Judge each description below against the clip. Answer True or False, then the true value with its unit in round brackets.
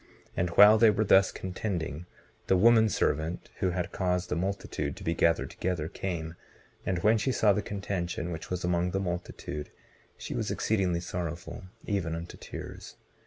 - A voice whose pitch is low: True (90 Hz)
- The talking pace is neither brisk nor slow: True (165 wpm)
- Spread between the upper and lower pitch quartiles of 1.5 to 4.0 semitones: True (2.7 semitones)